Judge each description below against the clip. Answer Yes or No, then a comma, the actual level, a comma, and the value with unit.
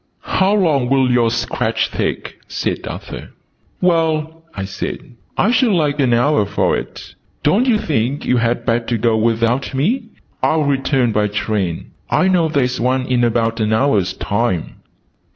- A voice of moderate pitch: No, low, 125 Hz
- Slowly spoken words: No, average, 155 wpm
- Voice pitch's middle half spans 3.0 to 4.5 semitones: No, wide, 5.4 semitones